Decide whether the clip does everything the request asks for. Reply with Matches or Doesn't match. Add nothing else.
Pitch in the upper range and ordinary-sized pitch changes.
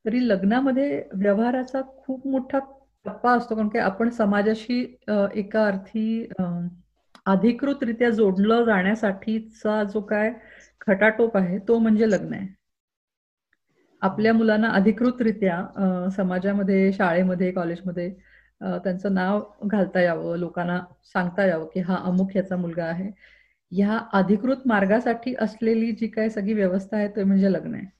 Matches